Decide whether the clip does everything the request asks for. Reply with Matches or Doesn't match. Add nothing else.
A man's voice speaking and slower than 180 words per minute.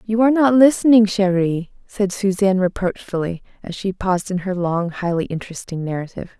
Doesn't match